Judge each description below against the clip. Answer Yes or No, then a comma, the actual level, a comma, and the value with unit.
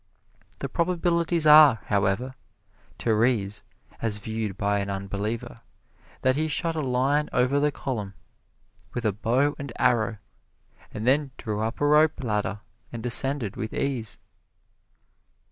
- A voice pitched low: Yes, low, 120 Hz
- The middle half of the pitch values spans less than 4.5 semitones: No, average, 5.3 semitones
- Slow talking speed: Yes, slow, 130 wpm